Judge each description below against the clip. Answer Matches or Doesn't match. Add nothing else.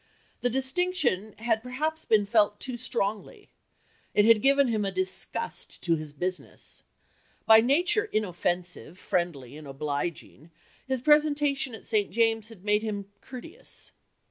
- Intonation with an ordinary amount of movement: Doesn't match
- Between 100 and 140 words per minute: Matches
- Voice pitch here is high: Matches